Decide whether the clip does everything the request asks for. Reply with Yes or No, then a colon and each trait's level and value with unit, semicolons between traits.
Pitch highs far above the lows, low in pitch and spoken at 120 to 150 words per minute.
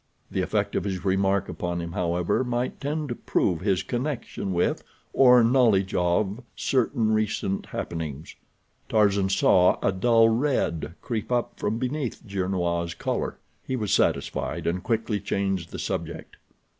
No: average, 4.8 semitones; low, 100 Hz; average, 145 wpm